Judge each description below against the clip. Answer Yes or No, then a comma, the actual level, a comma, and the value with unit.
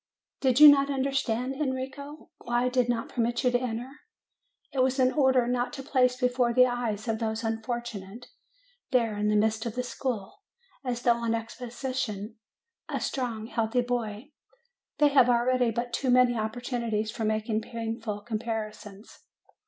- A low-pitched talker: No, high, 240 Hz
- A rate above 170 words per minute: No, average, 160 wpm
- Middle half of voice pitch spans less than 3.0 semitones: Yes, narrow, 2.4 semitones